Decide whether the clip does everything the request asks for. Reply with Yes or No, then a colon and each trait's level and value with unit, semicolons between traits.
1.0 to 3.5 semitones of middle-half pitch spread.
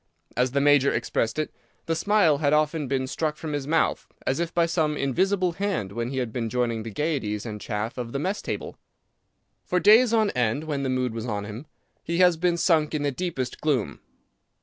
No: average, 5.3 semitones